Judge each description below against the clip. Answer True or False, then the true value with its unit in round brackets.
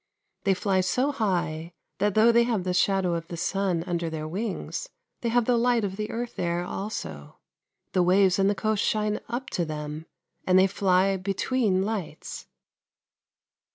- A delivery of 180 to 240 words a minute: False (170 wpm)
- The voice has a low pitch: False (195 Hz)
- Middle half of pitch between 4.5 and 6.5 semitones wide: False (3.6 semitones)